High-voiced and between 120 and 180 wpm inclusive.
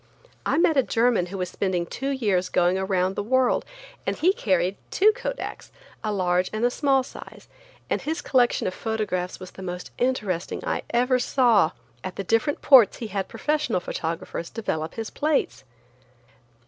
Yes: high, 215 Hz; average, 170 wpm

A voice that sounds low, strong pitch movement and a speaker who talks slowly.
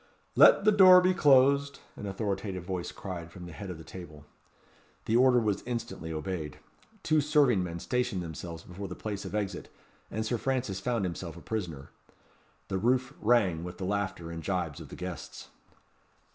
No: very low, 95 Hz; wide, 5.9 semitones; average, 175 wpm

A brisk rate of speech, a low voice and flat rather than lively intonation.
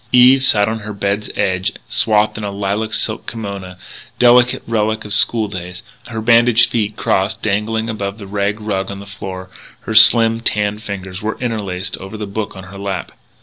No: average, 185 wpm; low, 105 Hz; narrow, 2.1 semitones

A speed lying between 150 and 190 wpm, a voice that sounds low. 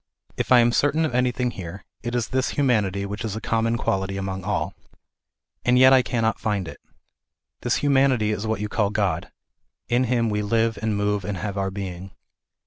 No: average, 200 wpm; low, 110 Hz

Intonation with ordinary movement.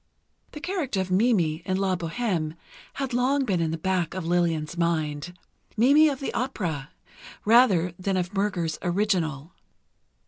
No: wide, 5.7 semitones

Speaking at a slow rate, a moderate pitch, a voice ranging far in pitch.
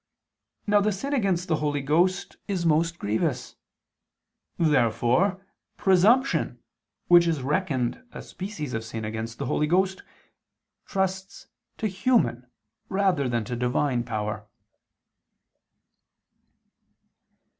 Yes: slow, 105 wpm; medium, 165 Hz; wide, 7.5 semitones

